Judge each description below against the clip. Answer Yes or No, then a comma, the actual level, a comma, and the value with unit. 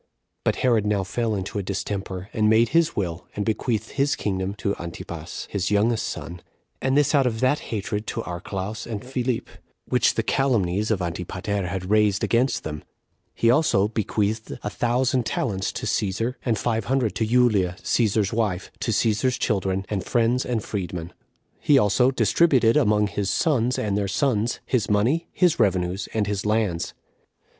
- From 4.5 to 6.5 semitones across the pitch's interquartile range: No, average, 3.7 semitones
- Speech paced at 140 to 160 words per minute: No, average, 170 wpm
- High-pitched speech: No, low, 105 Hz